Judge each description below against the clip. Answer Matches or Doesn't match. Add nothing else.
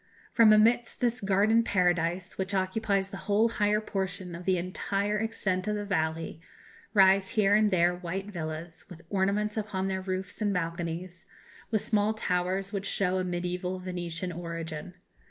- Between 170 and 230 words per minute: Doesn't match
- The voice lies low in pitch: Doesn't match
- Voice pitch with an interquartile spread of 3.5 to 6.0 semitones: Doesn't match